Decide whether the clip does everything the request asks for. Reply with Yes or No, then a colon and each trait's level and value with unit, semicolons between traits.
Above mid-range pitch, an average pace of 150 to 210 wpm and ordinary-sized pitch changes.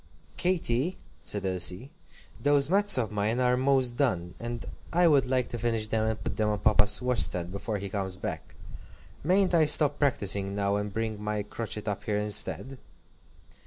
No: low, 115 Hz; average, 170 wpm; average, 4.7 semitones